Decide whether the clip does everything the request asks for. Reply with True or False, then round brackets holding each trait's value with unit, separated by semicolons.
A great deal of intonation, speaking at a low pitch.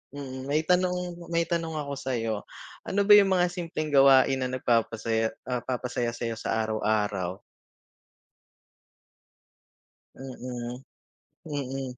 True (5.7 semitones; 130 Hz)